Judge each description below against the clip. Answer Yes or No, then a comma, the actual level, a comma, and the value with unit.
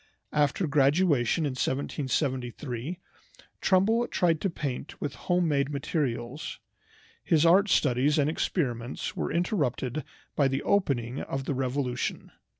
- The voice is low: No, medium, 145 Hz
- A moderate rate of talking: No, slow, 120 wpm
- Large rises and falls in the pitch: No, average, 4.2 semitones